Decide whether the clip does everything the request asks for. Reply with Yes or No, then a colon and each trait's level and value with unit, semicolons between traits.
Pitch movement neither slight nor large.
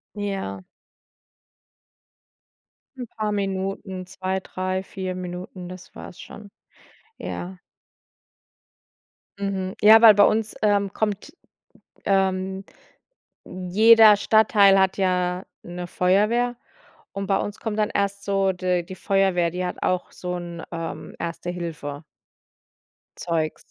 No: narrow, 2.1 semitones